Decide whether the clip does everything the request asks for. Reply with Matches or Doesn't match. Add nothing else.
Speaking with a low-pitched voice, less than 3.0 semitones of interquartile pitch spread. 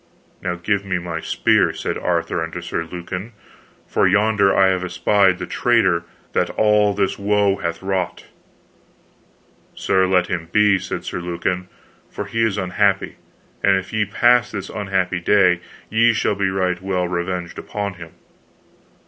Matches